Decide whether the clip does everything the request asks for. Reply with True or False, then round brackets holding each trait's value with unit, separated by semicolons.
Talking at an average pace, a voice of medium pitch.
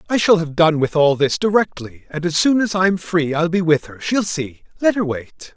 False (250 wpm; 170 Hz)